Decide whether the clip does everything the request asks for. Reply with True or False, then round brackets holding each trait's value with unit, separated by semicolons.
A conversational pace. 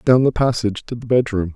False (230 wpm)